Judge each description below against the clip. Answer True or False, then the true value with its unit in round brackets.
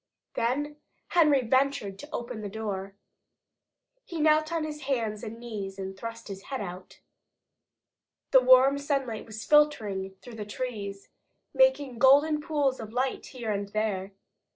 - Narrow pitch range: False (5.4 semitones)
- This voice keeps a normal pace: True (145 wpm)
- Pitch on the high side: True (240 Hz)